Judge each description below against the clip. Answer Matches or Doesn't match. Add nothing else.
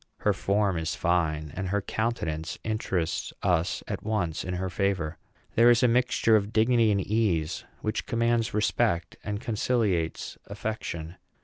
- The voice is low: Matches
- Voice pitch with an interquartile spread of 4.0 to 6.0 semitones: Matches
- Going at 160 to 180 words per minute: Doesn't match